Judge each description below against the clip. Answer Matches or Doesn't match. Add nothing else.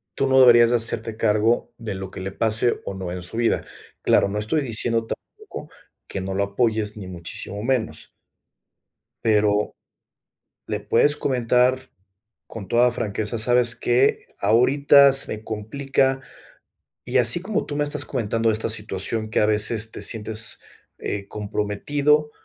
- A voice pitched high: Doesn't match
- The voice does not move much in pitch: Doesn't match